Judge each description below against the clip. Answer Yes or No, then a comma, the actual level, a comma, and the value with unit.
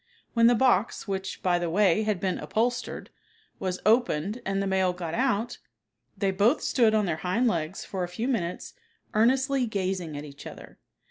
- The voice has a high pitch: Yes, high, 195 Hz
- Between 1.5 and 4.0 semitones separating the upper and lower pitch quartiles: No, average, 4.4 semitones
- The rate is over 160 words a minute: Yes, average, 180 wpm